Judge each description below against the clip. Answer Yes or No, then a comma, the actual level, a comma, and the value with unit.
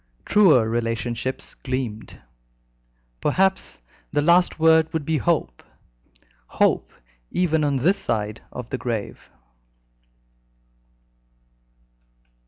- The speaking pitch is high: No, medium, 140 Hz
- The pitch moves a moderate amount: No, wide, 5.7 semitones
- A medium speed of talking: No, slow, 85 wpm